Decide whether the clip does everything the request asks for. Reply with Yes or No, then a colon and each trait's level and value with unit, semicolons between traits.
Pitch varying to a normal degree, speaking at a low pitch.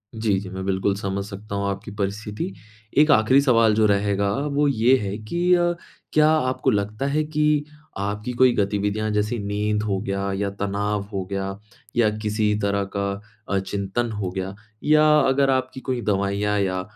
Yes: average, 4.0 semitones; low, 105 Hz